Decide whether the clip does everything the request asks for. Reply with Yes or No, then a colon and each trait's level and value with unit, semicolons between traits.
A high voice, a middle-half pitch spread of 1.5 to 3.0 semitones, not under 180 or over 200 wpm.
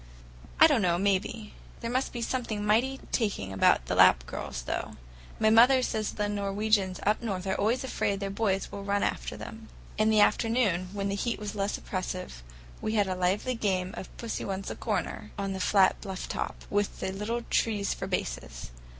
Yes: high, 205 Hz; average, 2.7 semitones; average, 190 wpm